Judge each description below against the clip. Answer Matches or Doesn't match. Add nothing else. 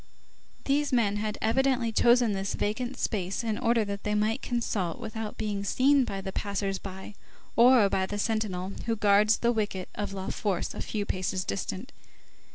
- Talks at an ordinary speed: Matches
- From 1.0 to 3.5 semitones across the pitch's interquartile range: Matches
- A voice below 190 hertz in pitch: Doesn't match